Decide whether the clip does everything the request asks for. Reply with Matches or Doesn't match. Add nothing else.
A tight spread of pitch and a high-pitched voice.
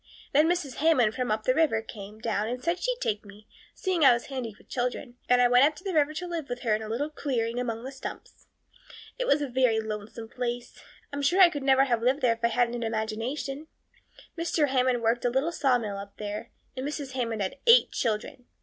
Doesn't match